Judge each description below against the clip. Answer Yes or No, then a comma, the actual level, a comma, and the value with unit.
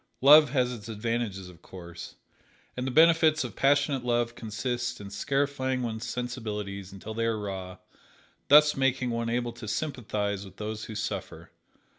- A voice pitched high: No, low, 120 Hz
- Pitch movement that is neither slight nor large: Yes, average, 4.1 semitones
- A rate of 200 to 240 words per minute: No, average, 155 wpm